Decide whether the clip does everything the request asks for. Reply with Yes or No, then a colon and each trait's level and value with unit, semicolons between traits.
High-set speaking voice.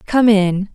Yes: high, 205 Hz